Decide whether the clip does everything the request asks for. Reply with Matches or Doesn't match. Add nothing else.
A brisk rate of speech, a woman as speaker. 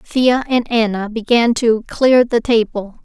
Doesn't match